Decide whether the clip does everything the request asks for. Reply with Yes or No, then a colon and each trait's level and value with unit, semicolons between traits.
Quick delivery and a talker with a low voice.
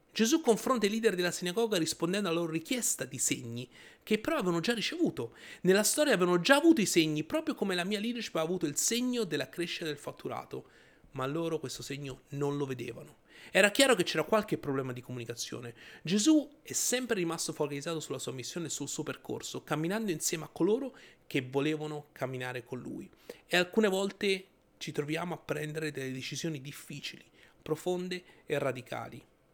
No: fast, 175 wpm; medium, 165 Hz